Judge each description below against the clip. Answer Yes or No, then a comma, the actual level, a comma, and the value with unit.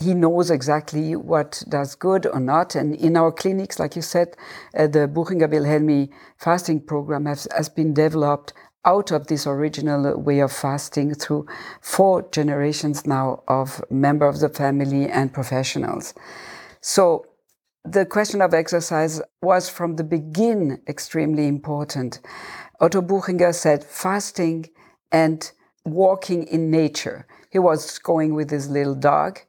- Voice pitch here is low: No, medium, 155 Hz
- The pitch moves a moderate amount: Yes, average, 3.0 semitones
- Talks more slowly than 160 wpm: Yes, average, 140 wpm